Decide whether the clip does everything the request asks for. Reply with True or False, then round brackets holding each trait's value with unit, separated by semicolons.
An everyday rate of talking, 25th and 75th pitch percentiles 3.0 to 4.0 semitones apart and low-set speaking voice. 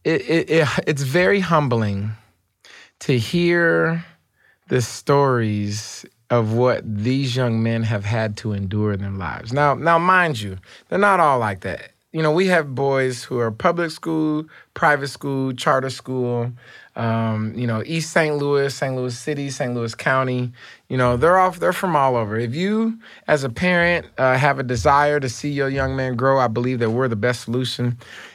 False (180 wpm; 4.6 semitones; 130 Hz)